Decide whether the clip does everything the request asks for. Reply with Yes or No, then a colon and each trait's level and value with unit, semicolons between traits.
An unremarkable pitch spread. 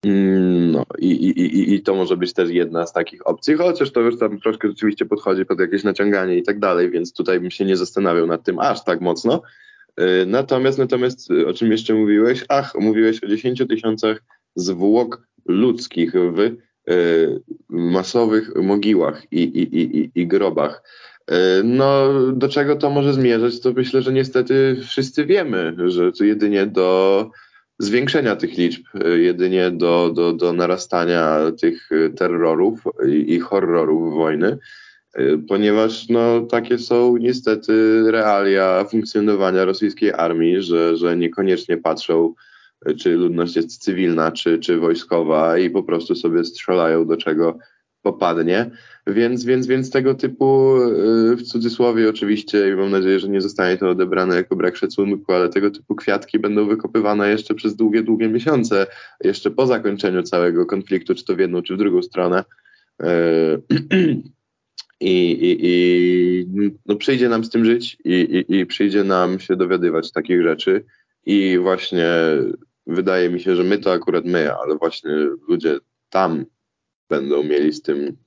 No: wide, 6.1 semitones